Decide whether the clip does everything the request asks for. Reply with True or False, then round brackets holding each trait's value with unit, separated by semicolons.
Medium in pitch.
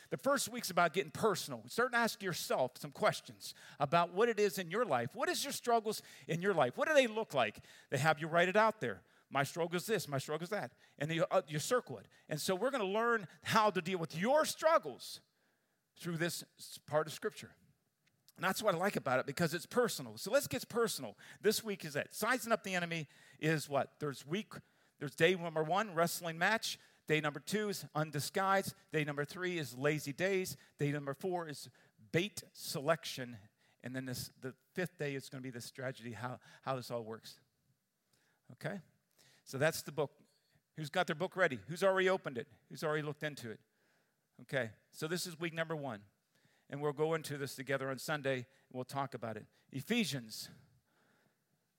True (160 Hz)